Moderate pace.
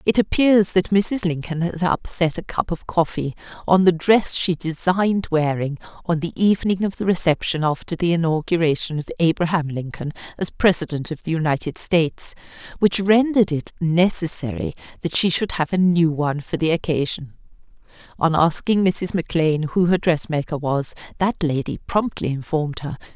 Yes: average, 165 wpm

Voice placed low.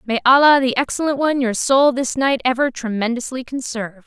No: very high, 255 Hz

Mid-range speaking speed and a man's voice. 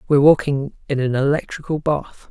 Yes: average, 155 wpm; male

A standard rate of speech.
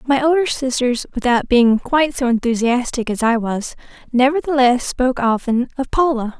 Yes: average, 150 wpm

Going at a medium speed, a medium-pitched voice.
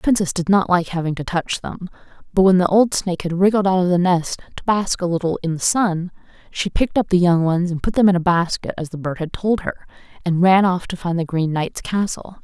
No: fast, 260 wpm; medium, 180 Hz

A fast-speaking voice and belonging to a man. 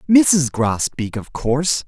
No: slow, 130 wpm; male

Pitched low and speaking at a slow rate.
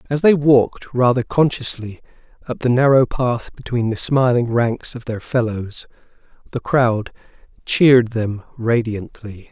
Yes: low, 120 Hz; slow, 130 wpm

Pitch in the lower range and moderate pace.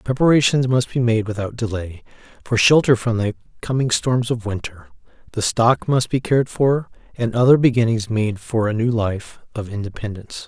Yes: low, 115 Hz; average, 170 wpm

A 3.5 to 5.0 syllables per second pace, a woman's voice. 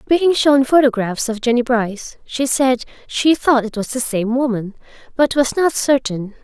Yes: 4.5 syllables/s; female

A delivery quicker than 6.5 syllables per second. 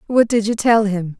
No: 4.9 syllables/s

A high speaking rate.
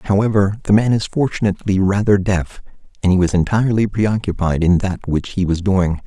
No: average, 180 wpm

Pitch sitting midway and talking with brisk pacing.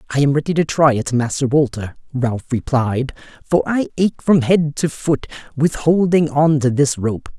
No: medium, 145 Hz; average, 185 wpm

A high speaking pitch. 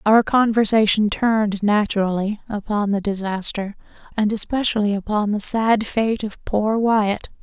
Yes: high, 210 Hz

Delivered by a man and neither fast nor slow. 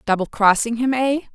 No: female; average, 180 wpm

